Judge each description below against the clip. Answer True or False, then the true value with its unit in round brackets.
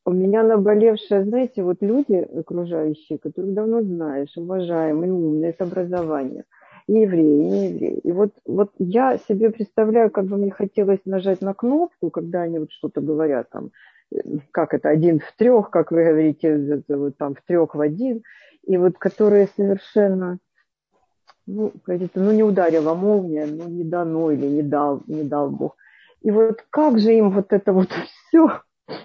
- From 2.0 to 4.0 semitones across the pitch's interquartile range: False (4.7 semitones)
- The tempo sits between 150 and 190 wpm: True (160 wpm)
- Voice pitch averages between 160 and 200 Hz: True (185 Hz)